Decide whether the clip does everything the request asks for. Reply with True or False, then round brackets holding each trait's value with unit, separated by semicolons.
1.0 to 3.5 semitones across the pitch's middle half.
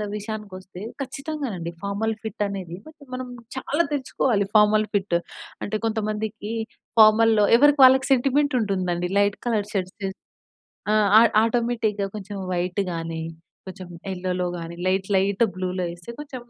False (4.0 semitones)